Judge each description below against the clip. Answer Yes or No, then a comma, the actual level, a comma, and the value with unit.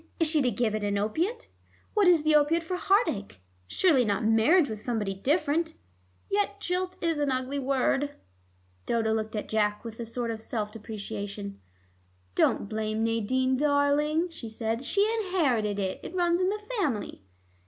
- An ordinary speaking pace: Yes, average, 170 wpm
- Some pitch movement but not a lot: No, wide, 7.1 semitones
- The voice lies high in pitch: Yes, very high, 255 Hz